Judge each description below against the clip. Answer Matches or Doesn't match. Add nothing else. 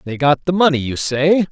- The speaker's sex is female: Doesn't match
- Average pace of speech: Doesn't match